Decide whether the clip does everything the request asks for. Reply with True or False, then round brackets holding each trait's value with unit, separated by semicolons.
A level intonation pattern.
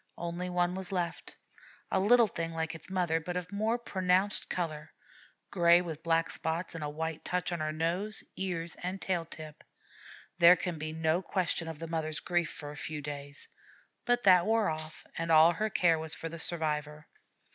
True (2.3 semitones)